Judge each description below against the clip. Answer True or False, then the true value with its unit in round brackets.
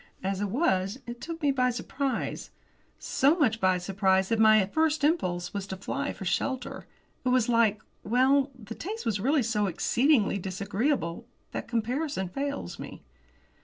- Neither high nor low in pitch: False (230 Hz)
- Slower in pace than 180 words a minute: True (160 wpm)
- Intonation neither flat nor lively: False (6.0 semitones)